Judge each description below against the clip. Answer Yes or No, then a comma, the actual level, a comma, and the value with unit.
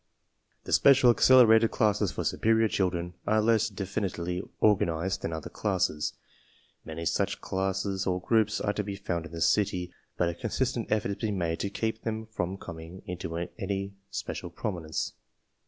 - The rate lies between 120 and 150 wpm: No, average, 165 wpm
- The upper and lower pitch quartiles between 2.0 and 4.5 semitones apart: Yes, average, 3.8 semitones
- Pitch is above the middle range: No, very low, 95 Hz